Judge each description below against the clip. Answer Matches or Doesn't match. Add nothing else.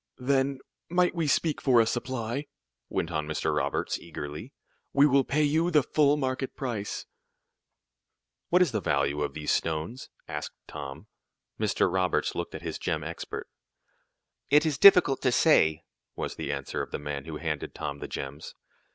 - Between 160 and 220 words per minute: Matches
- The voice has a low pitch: Matches